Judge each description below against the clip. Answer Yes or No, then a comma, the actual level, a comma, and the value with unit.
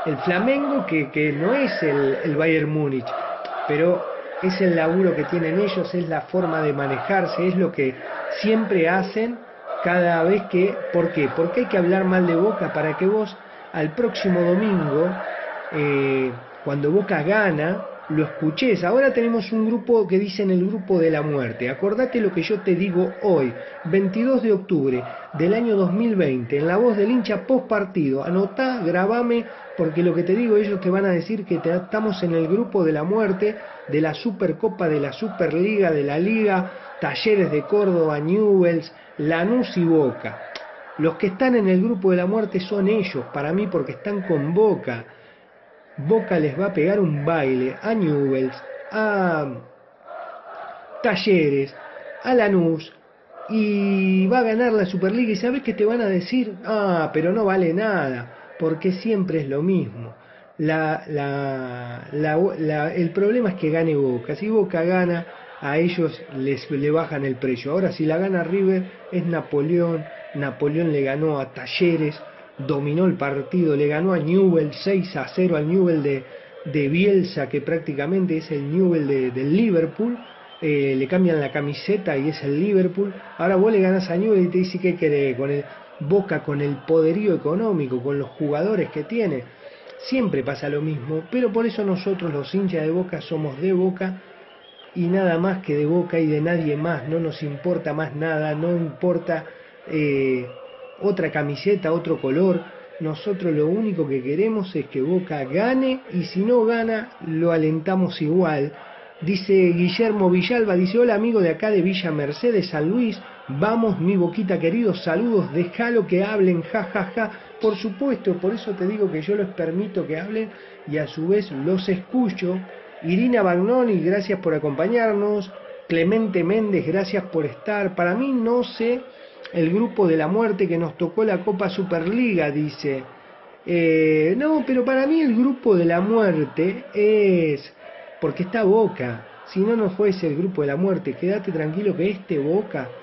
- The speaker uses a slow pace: No, average, 170 wpm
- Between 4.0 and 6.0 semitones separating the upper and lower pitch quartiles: Yes, average, 4.8 semitones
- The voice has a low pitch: No, medium, 180 Hz